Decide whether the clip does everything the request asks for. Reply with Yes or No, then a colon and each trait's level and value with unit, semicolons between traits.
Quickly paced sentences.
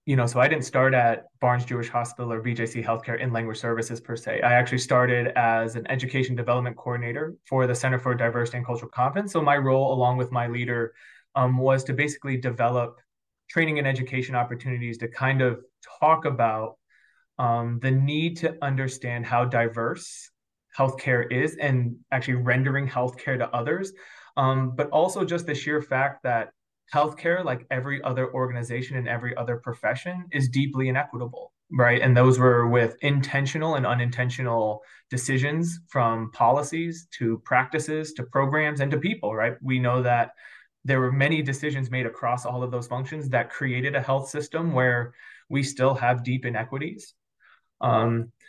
No: average, 165 wpm